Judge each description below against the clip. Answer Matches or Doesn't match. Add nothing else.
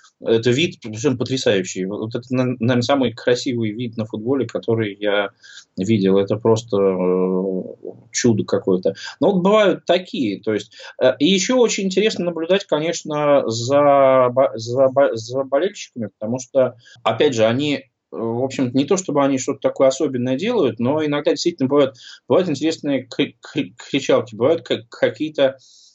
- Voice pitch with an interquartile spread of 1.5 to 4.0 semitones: Doesn't match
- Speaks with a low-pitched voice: Matches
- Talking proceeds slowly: Doesn't match